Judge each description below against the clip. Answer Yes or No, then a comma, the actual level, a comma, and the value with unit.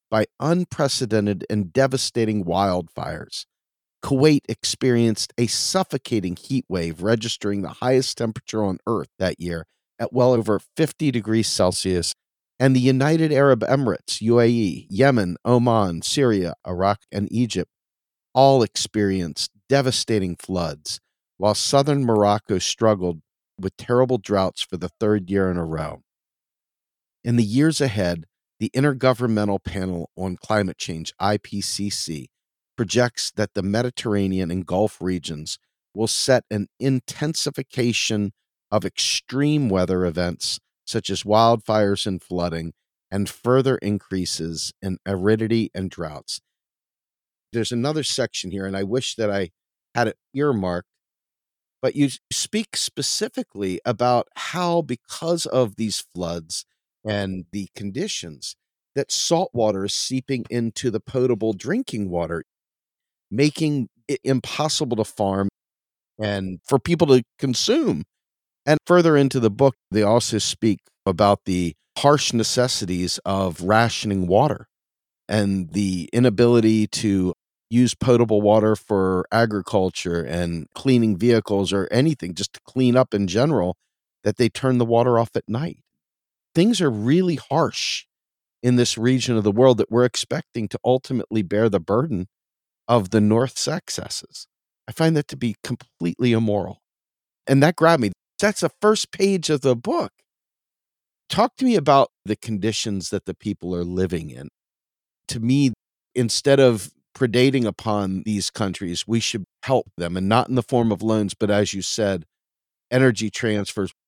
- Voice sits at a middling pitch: No, low, 110 Hz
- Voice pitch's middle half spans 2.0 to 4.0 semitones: No, average, 4.8 semitones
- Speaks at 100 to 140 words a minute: Yes, slow, 135 wpm